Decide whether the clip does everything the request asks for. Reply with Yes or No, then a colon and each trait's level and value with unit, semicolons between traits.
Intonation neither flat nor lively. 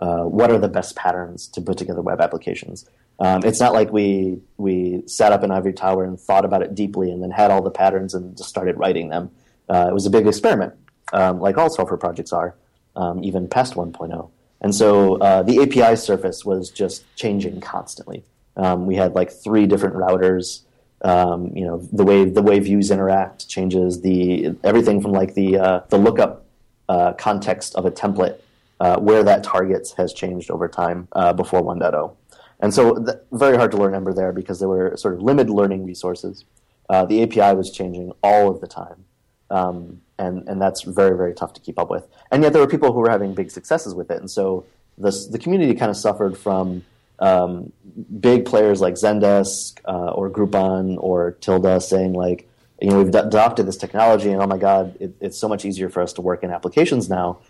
No: narrow, 2.0 semitones